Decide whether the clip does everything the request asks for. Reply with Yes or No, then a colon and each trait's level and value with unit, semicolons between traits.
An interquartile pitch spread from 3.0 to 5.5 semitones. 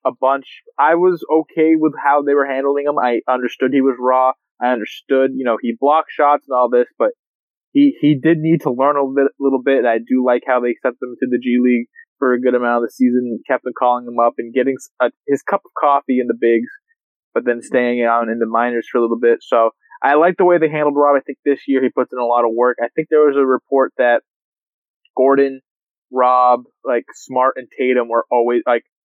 No: narrow, 2.6 semitones